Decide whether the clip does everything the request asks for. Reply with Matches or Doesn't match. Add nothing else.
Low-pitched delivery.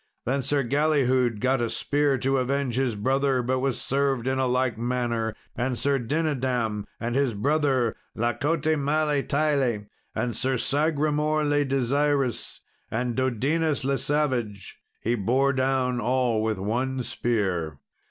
Matches